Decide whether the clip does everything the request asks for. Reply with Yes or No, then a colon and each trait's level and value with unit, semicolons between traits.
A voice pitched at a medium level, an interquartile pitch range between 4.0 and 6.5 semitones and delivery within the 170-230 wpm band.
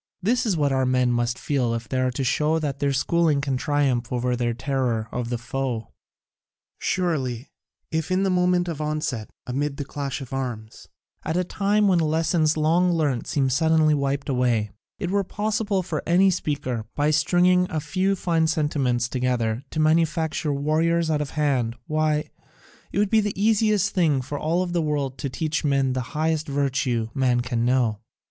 Yes: medium, 145 Hz; average, 4.7 semitones; average, 180 wpm